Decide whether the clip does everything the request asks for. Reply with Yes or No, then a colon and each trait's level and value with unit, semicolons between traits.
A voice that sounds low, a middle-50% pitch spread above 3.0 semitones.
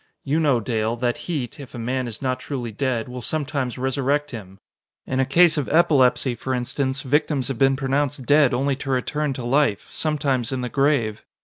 No: low, 130 Hz; narrow, 2.6 semitones